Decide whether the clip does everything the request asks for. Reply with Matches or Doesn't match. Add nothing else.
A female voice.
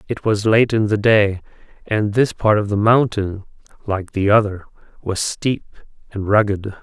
Doesn't match